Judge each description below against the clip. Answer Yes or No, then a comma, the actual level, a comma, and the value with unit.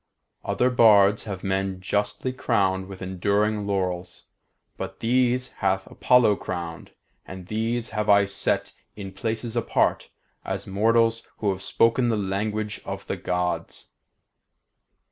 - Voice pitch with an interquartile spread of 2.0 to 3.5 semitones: Yes, average, 2.9 semitones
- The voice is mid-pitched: No, low, 100 Hz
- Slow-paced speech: Yes, slow, 125 wpm